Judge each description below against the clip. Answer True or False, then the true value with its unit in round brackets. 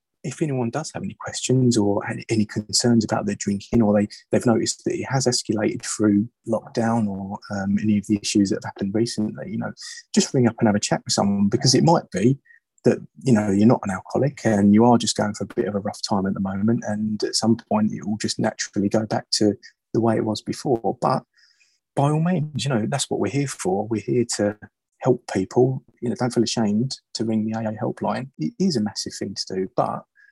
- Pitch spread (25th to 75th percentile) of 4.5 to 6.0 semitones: False (3.5 semitones)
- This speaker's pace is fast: True (240 wpm)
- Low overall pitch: True (115 Hz)